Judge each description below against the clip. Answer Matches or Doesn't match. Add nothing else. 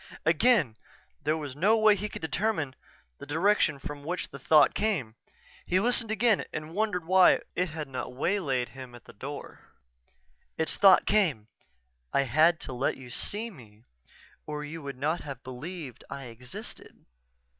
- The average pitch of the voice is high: Doesn't match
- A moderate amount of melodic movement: Doesn't match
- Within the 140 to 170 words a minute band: Matches